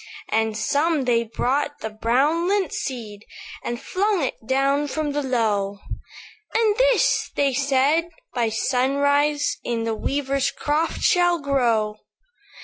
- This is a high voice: Yes, very high, 275 Hz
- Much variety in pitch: No, average, 4.2 semitones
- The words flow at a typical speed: No, slow, 130 wpm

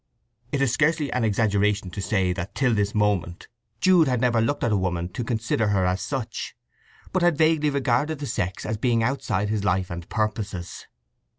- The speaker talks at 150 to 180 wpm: No, average, 190 wpm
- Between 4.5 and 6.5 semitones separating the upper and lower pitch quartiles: Yes, wide, 5.5 semitones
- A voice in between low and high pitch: No, low, 110 Hz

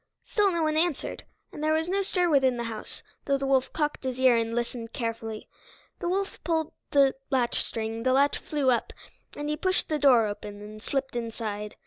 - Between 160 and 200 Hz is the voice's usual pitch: No, very high, 265 Hz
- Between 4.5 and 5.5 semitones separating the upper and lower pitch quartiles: Yes, average, 5.1 semitones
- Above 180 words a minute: Yes, average, 195 wpm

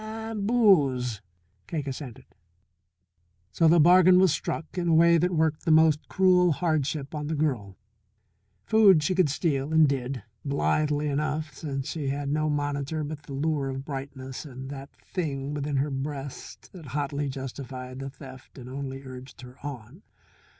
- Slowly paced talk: No, average, 160 wpm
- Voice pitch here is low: No, medium, 145 Hz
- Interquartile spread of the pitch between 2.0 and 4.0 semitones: Yes, average, 2.9 semitones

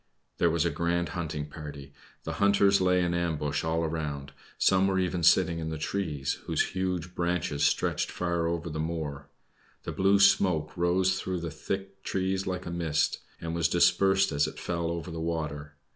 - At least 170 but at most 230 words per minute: Yes, average, 180 wpm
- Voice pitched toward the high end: No, very low, 85 Hz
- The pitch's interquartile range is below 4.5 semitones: Yes, average, 3.0 semitones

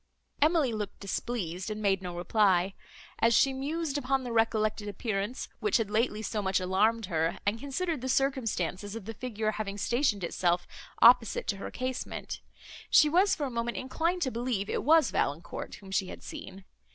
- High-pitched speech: Yes, high, 225 Hz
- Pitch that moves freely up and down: No, average, 4.9 semitones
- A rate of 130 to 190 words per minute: Yes, average, 175 wpm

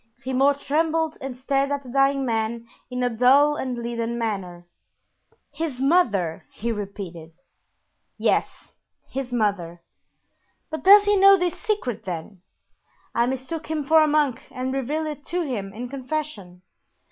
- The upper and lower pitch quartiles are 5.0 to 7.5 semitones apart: Yes, average, 5.3 semitones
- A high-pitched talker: Yes, very high, 260 Hz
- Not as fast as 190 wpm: Yes, average, 145 wpm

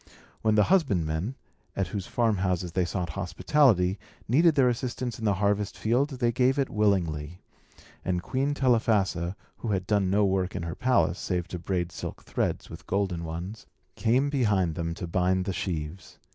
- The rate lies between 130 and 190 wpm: Yes, average, 170 wpm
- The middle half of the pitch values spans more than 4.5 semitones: Yes, average, 4.9 semitones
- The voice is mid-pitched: No, low, 100 Hz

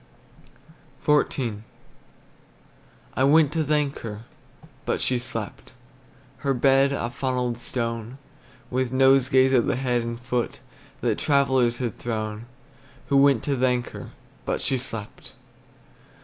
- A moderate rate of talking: No, slow, 120 wpm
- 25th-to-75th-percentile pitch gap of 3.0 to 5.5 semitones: No, narrow, 2.5 semitones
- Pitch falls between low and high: No, low, 125 Hz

